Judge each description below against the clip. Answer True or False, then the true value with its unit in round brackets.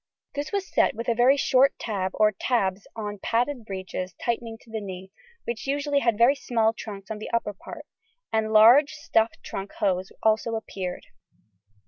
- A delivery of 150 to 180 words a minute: True (170 wpm)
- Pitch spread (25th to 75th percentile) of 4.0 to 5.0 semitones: False (3.3 semitones)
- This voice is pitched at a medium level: False (220 Hz)